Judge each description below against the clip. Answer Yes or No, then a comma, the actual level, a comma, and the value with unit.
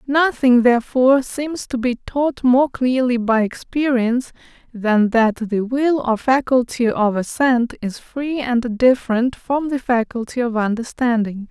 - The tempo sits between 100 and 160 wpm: Yes, average, 140 wpm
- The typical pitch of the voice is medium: No, high, 245 Hz